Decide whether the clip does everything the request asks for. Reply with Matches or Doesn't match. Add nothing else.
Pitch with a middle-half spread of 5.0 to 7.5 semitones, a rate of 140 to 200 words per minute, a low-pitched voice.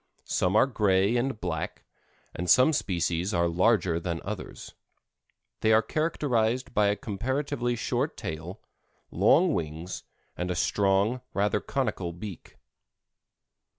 Doesn't match